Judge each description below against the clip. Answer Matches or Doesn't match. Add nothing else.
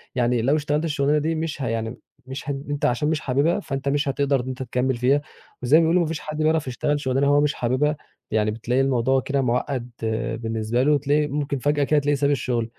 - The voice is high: Doesn't match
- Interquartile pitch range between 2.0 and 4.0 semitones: Matches